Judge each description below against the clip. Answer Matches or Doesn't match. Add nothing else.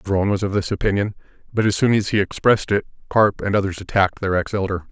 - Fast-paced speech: Matches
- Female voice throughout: Doesn't match